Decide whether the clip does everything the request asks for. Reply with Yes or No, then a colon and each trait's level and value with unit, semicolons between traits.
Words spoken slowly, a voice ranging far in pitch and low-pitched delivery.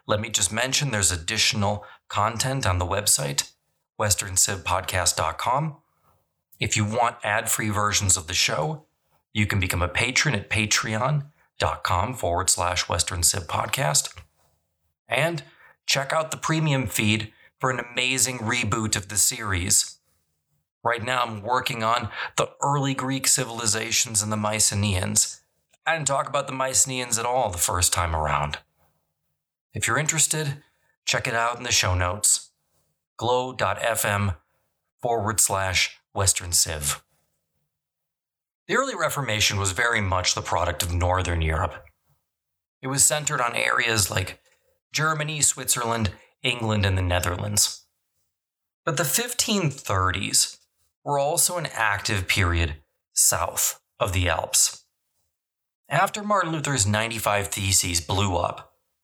Yes: slow, 125 wpm; wide, 6.4 semitones; low, 105 Hz